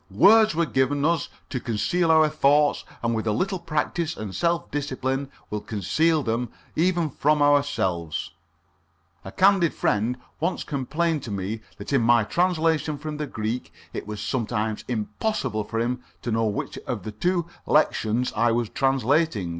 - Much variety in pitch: Yes, wide, 6.3 semitones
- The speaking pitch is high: No, low, 135 Hz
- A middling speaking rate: Yes, average, 160 wpm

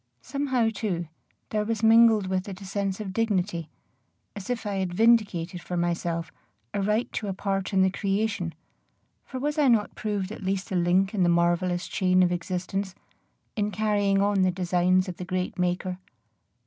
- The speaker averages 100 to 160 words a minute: No, average, 180 wpm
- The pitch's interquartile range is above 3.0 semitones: No, average, 2.7 semitones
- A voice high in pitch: Yes, high, 195 Hz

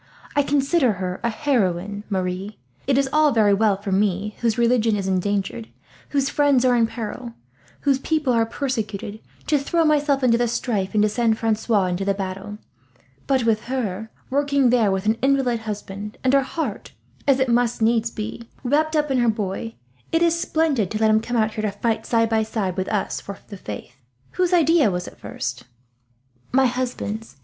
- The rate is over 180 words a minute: Yes, average, 190 wpm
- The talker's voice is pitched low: No, high, 225 Hz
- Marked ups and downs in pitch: No, average, 4.6 semitones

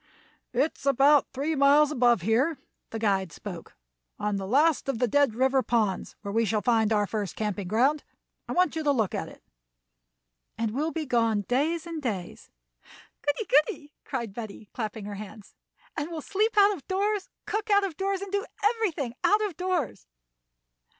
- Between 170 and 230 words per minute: Yes, average, 180 wpm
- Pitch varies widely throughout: Yes, wide, 6.9 semitones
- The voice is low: No, very high, 265 Hz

